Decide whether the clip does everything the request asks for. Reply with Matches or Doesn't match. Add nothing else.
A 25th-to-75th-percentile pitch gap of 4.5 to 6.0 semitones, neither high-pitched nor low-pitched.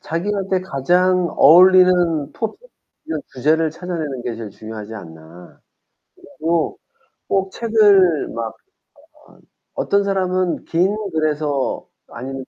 Matches